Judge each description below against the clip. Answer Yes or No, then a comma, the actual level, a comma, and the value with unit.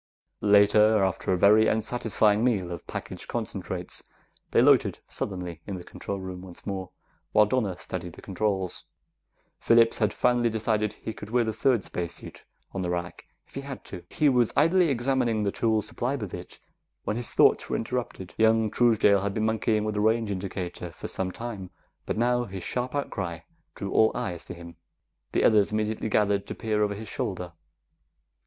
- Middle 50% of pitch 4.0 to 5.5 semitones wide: No, average, 3.4 semitones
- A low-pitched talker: Yes, low, 105 Hz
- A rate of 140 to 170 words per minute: No, average, 180 wpm